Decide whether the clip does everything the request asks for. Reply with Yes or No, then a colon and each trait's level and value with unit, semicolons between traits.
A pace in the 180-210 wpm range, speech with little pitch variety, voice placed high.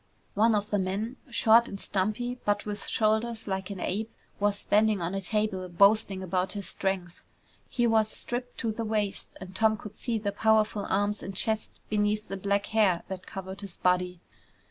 Yes: average, 185 wpm; narrow, 2.3 semitones; high, 205 Hz